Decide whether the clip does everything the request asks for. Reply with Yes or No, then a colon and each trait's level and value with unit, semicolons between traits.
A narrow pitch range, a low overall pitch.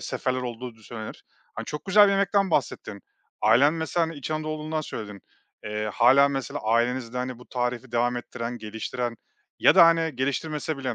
No: average, 4.7 semitones; low, 130 Hz